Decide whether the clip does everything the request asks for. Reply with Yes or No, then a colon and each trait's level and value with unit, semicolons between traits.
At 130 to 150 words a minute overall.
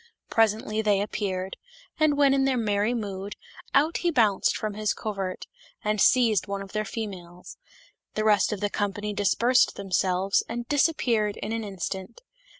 No: average, 160 wpm